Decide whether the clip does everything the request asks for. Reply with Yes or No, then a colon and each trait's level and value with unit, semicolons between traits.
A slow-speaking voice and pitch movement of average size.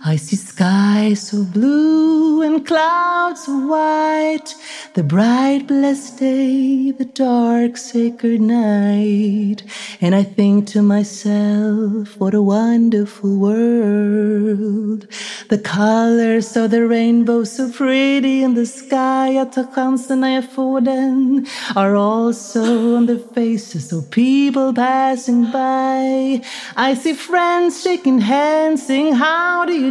Yes: slow, 120 wpm; average, 4.2 semitones